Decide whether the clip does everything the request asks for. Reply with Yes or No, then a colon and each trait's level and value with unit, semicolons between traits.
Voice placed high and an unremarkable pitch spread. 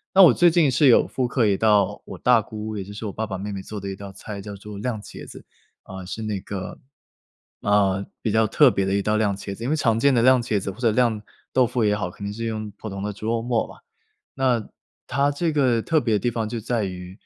No: low, 110 Hz; average, 3.3 semitones